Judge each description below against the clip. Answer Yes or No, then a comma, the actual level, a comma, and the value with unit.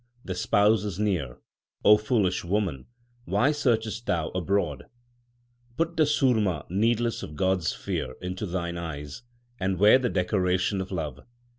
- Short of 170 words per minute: Yes, average, 150 wpm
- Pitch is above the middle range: No, very low, 95 Hz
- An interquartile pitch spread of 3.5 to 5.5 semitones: Yes, average, 4.0 semitones